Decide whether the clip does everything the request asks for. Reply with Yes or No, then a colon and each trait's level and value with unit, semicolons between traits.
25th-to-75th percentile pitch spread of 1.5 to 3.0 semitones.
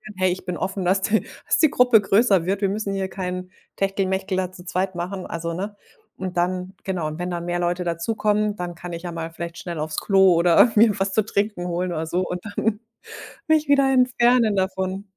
Yes: average, 2.7 semitones